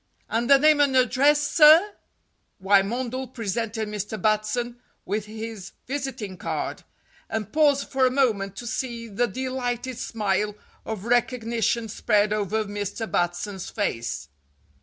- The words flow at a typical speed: No, slow, 125 wpm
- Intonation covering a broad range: No, average, 3.8 semitones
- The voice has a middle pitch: No, high, 225 Hz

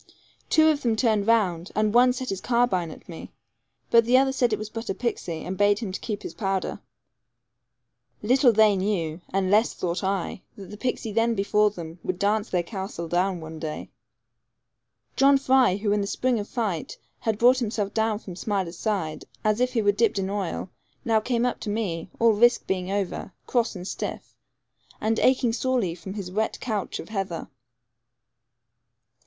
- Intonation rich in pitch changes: No, average, 3.6 semitones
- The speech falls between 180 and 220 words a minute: Yes, average, 185 wpm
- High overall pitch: Yes, high, 210 Hz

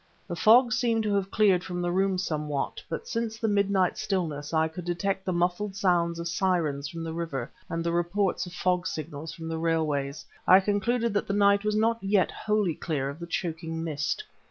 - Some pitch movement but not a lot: Yes, average, 3.6 semitones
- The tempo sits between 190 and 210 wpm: Yes, fast, 205 wpm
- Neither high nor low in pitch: Yes, medium, 175 Hz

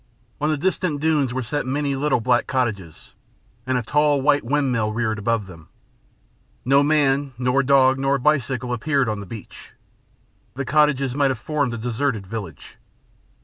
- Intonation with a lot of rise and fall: No, average, 3.6 semitones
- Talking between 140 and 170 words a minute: Yes, average, 160 wpm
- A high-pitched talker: No, low, 130 Hz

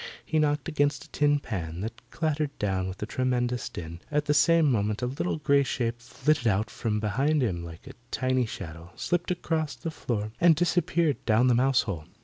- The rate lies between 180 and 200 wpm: Yes, average, 195 wpm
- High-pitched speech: No, low, 130 Hz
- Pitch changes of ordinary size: No, wide, 5.9 semitones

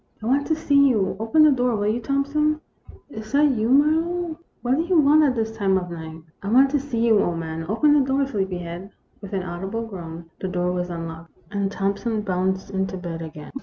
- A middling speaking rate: No, fast, 240 wpm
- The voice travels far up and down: Yes, wide, 7.4 semitones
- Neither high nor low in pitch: No, high, 215 Hz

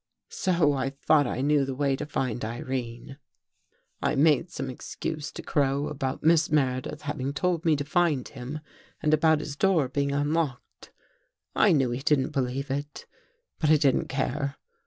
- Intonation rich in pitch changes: No, narrow, 2.4 semitones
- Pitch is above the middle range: No, medium, 140 Hz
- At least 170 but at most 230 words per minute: Yes, average, 175 wpm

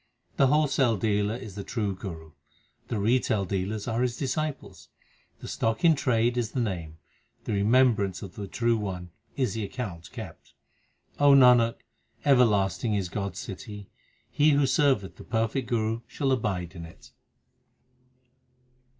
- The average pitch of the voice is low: Yes, low, 110 Hz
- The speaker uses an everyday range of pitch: Yes, average, 4.3 semitones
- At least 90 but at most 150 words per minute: Yes, average, 145 wpm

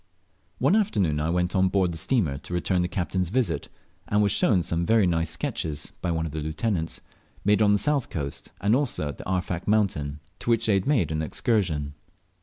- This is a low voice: Yes, very low, 90 Hz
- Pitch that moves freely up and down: No, average, 4.7 semitones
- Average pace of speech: No, fast, 210 wpm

